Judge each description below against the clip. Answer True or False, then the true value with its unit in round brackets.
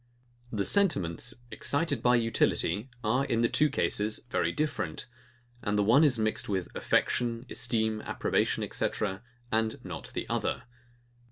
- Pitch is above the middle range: False (115 Hz)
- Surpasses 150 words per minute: False (140 wpm)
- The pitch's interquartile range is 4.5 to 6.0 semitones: False (3.4 semitones)